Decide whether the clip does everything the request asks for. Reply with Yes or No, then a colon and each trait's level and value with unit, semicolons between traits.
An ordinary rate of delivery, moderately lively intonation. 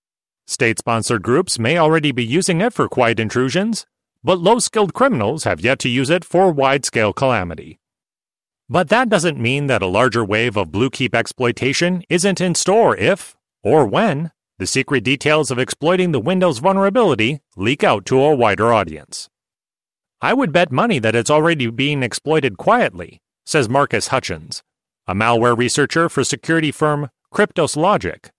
No: average, 150 wpm; wide, 6.8 semitones